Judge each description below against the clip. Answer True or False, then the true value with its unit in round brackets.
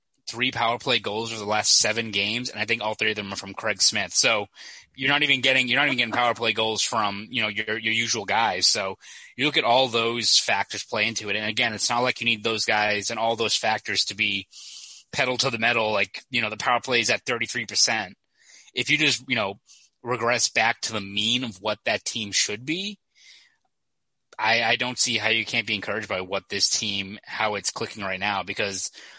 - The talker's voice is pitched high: False (115 Hz)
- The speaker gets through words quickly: True (230 wpm)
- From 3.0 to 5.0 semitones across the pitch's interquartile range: False (2.6 semitones)